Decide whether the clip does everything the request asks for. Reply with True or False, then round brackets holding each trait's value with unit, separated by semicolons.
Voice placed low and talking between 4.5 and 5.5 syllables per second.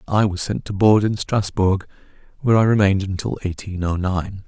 True (100 Hz; 5.4 syllables/s)